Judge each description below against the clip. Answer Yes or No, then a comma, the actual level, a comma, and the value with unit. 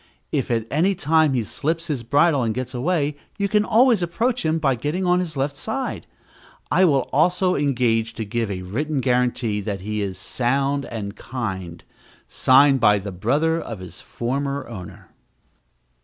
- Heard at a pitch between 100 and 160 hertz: Yes, low, 135 Hz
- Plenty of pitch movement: Yes, wide, 6.1 semitones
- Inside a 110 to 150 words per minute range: No, average, 170 wpm